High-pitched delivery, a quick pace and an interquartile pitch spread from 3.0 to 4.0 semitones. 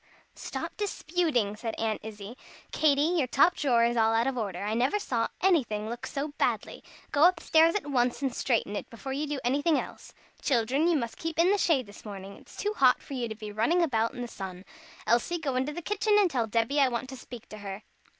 No: very high, 255 Hz; fast, 230 wpm; wide, 5.6 semitones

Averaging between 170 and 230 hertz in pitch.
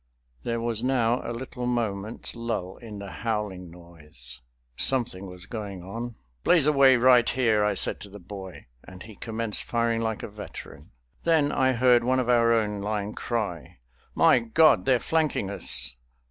No: low, 115 Hz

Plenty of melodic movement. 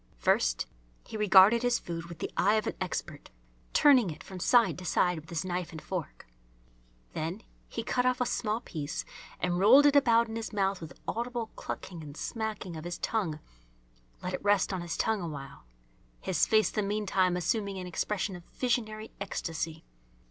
No: average, 4.5 semitones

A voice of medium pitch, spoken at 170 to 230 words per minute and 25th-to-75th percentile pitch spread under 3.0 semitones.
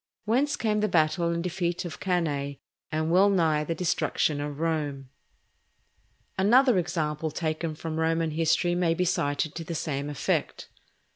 No: medium, 165 Hz; average, 150 wpm; narrow, 2.6 semitones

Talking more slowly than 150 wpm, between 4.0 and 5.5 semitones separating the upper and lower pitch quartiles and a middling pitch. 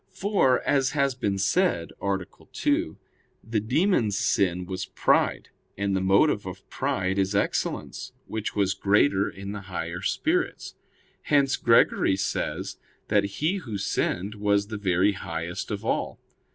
No: average, 140 wpm; average, 4.7 semitones; low, 100 Hz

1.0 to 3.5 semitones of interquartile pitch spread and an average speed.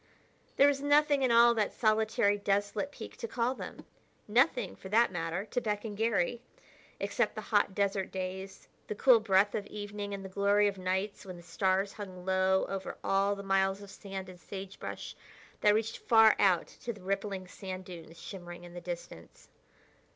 Yes: narrow, 2.4 semitones; average, 180 wpm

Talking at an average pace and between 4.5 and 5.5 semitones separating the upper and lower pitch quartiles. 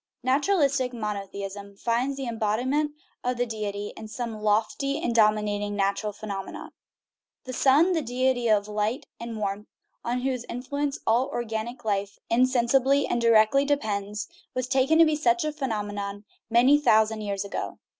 No: average, 145 wpm; average, 4.1 semitones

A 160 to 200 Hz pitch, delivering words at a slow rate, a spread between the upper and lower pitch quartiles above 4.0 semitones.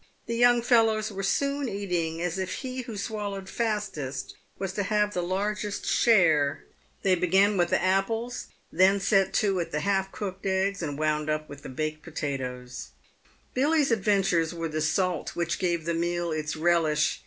No: high, 190 Hz; average, 165 wpm; average, 4.4 semitones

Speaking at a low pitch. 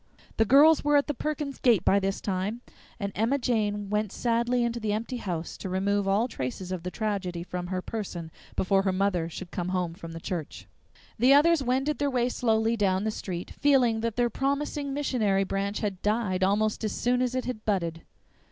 No: high, 210 Hz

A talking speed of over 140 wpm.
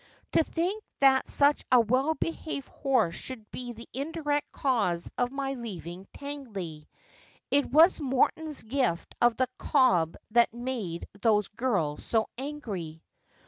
No: slow, 135 wpm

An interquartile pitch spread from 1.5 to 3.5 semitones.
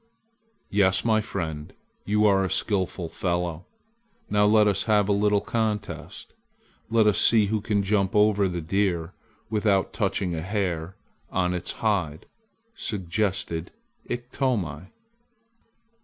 Yes: average, 2.9 semitones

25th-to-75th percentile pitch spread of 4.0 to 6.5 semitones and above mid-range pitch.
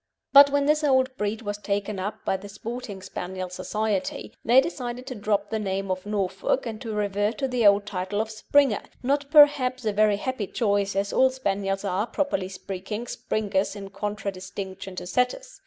Yes: average, 4.3 semitones; high, 210 Hz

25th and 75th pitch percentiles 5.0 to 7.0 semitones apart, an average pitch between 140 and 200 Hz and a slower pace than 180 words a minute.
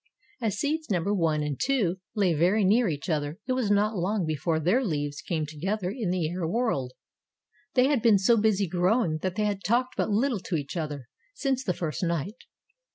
No: wide, 5.5 semitones; high, 190 Hz; average, 200 wpm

